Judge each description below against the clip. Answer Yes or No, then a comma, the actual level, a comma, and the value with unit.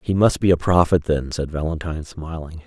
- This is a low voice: Yes, very low, 80 Hz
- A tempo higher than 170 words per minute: Yes, fast, 205 wpm